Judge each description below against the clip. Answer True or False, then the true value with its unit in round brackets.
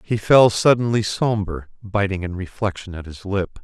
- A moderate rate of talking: True (165 wpm)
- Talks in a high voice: False (100 Hz)